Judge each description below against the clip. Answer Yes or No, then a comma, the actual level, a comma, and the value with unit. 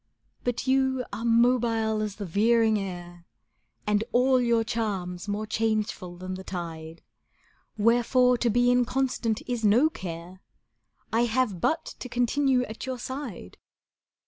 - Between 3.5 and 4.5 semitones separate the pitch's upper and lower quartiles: Yes, average, 4.0 semitones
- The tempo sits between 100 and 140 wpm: Yes, slow, 135 wpm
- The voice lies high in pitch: Yes, high, 225 Hz